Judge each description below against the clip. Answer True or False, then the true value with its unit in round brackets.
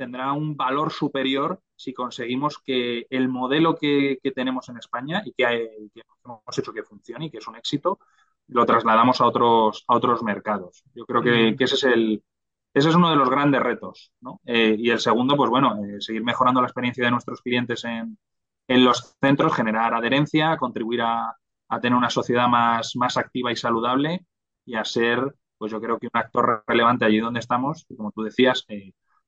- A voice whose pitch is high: False (120 Hz)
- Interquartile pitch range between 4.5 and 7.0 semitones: False (2.5 semitones)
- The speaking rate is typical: False (200 wpm)